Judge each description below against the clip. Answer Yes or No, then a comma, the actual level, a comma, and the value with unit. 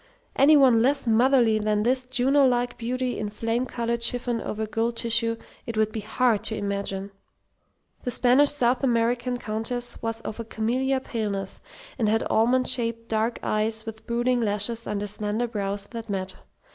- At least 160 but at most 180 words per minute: Yes, average, 165 wpm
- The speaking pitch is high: Yes, high, 230 Hz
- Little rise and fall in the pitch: Yes, narrow, 2.3 semitones